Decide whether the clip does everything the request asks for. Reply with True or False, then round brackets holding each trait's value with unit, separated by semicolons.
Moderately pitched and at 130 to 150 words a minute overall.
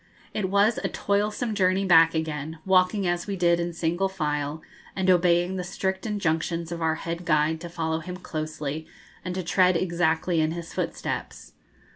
False (170 Hz; 170 wpm)